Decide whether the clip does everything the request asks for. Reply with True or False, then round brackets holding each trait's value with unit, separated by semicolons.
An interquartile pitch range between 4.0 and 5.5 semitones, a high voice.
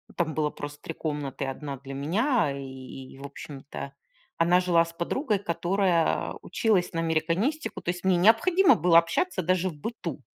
False (4.4 semitones; 170 Hz)